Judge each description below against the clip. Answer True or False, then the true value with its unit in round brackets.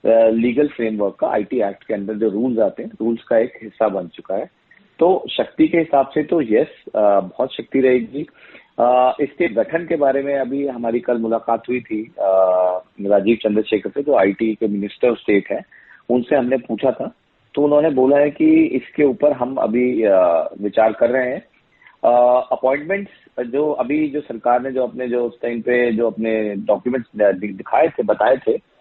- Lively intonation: False (3.7 semitones)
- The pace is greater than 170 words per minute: True (185 wpm)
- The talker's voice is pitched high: False (120 Hz)